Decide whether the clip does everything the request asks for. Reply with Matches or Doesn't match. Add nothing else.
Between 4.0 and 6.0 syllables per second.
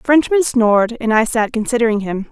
Matches